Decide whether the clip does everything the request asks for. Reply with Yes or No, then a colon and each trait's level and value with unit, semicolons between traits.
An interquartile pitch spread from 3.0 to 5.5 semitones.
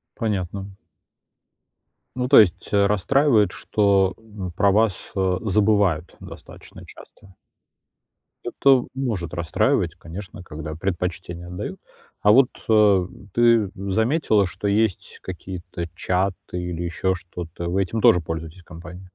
Yes: average, 3.3 semitones